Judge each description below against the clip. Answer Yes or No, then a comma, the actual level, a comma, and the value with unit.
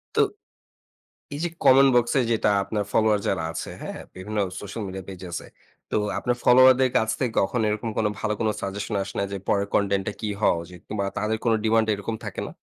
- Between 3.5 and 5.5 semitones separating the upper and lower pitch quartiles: No, narrow, 2.5 semitones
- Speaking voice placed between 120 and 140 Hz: No, low, 105 Hz